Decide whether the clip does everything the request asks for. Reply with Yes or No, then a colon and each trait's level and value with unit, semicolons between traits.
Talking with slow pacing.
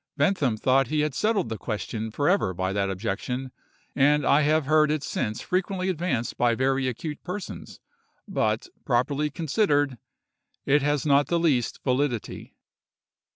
No: average, 150 wpm